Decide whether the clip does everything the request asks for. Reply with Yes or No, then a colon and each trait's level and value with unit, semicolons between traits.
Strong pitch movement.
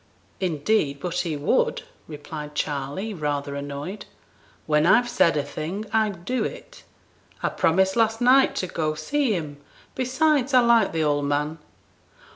Yes: wide, 7.2 semitones